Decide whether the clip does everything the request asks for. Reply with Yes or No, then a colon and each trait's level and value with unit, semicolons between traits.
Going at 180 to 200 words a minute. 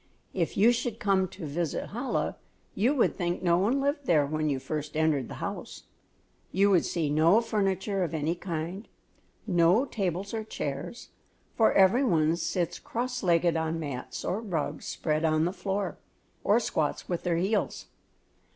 No: average, 165 wpm